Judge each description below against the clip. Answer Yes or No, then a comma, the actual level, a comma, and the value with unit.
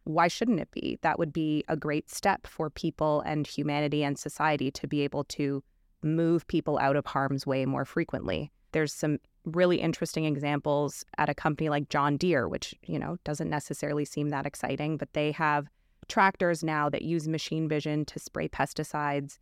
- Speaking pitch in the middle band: Yes, medium, 150 Hz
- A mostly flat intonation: Yes, narrow, 1.6 semitones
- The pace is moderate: Yes, average, 180 wpm